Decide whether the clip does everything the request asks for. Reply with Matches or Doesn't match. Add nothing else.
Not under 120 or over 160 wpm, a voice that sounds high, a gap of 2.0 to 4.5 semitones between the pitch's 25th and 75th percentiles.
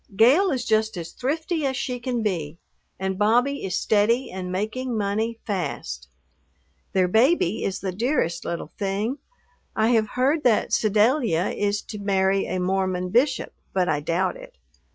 Doesn't match